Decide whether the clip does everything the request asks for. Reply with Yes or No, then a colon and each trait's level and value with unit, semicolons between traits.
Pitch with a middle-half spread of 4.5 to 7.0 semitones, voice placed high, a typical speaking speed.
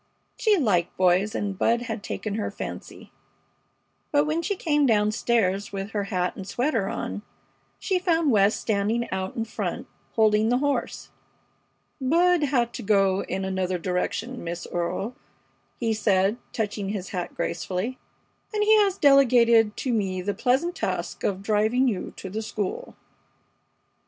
Yes: average, 4.8 semitones; high, 215 Hz; average, 150 wpm